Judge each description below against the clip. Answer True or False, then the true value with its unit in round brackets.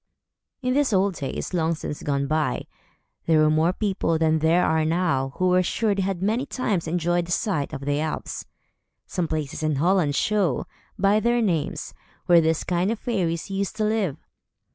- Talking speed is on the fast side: False (185 wpm)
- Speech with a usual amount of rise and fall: True (4.0 semitones)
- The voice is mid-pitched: True (175 Hz)